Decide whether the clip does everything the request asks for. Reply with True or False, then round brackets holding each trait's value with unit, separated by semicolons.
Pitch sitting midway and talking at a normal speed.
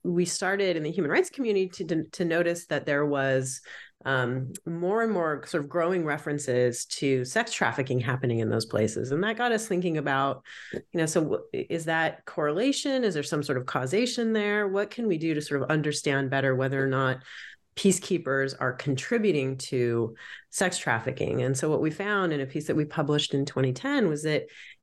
True (155 Hz; 195 wpm)